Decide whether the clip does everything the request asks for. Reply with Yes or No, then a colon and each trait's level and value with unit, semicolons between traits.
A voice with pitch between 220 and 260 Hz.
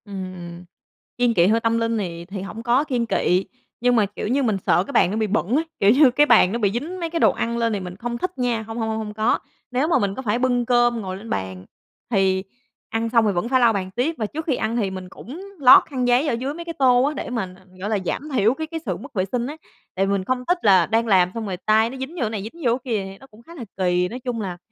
Yes: high, 230 Hz